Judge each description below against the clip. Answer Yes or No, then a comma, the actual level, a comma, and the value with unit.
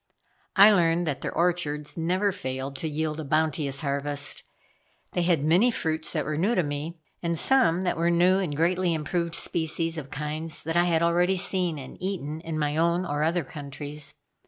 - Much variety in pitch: No, average, 2.7 semitones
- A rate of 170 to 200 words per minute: Yes, average, 185 wpm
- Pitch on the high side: No, medium, 165 Hz